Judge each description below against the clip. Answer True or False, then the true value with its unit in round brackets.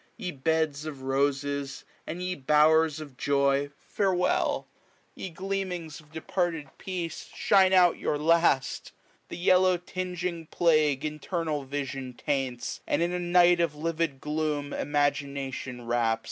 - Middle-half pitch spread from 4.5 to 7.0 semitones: False (3.7 semitones)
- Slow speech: True (130 wpm)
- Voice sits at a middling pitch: True (155 Hz)